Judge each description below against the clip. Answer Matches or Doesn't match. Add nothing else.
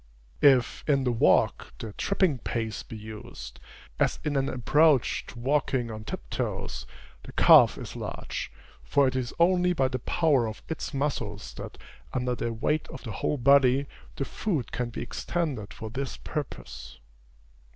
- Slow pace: Doesn't match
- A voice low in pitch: Matches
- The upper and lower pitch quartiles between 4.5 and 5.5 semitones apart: Doesn't match